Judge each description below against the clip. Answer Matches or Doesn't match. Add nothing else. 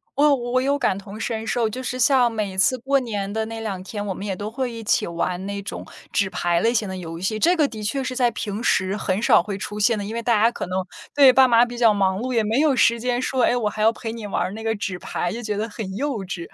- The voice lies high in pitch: Matches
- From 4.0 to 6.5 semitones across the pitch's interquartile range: Doesn't match